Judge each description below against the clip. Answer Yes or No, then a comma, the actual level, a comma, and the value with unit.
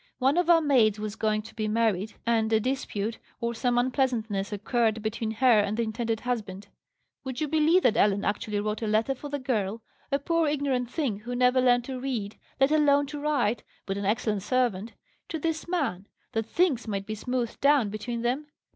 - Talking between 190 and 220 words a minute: Yes, average, 200 wpm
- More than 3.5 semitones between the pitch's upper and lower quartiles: Yes, average, 4.1 semitones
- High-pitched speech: Yes, high, 235 Hz